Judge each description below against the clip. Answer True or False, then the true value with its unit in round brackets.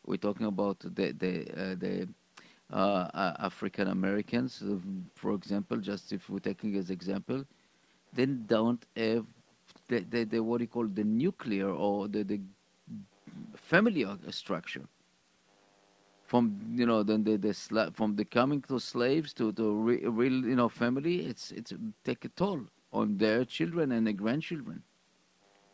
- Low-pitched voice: True (110 Hz)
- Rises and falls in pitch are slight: False (3.2 semitones)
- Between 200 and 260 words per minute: False (145 wpm)